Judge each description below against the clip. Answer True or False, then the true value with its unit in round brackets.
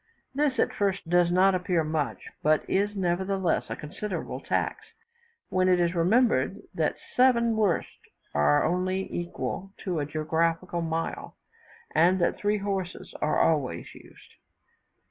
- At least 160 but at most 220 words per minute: False (135 wpm)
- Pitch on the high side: False (180 Hz)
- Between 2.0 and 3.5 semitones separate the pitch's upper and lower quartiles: True (3.0 semitones)